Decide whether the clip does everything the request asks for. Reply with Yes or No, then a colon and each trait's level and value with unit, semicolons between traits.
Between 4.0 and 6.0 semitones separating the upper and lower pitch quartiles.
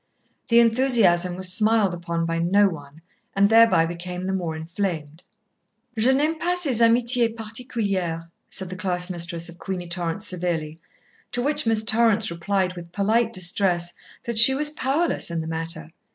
Yes: average, 5.1 semitones